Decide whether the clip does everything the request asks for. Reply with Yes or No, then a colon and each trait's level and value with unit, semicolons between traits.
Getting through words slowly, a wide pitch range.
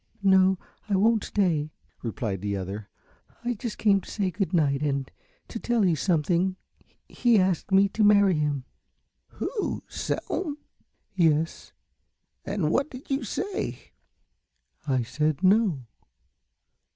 Yes: slow, 125 wpm; wide, 5.9 semitones